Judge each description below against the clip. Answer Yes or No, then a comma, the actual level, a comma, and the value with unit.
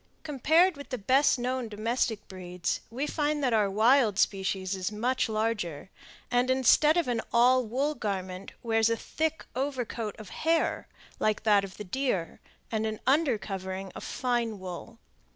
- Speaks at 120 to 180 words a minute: Yes, average, 165 wpm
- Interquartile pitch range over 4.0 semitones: Yes, average, 4.6 semitones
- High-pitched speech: Yes, high, 230 Hz